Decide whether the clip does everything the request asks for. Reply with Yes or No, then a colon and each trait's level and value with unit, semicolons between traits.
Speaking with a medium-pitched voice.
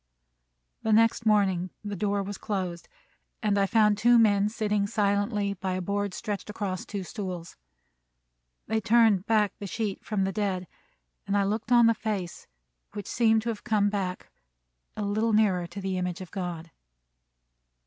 No: high, 205 Hz